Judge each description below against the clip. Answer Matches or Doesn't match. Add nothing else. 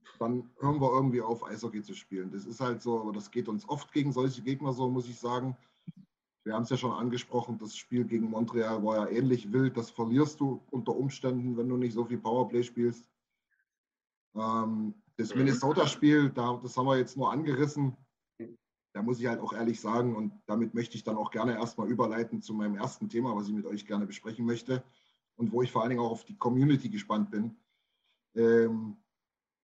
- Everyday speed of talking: Doesn't match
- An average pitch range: Doesn't match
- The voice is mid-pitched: Doesn't match